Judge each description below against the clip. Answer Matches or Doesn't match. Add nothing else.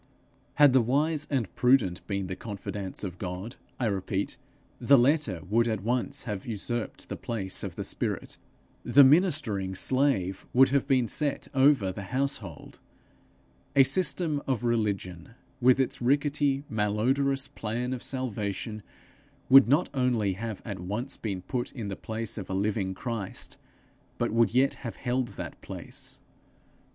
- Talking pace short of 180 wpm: Matches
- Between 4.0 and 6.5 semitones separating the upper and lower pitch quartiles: Matches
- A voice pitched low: Matches